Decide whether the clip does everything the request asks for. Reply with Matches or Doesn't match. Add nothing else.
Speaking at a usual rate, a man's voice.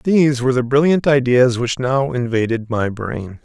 Matches